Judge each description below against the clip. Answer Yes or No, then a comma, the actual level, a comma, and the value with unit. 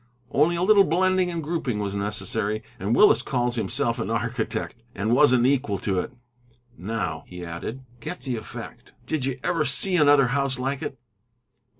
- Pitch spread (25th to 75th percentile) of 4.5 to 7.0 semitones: Yes, wide, 5.6 semitones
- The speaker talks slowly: No, average, 170 wpm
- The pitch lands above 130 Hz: No, low, 125 Hz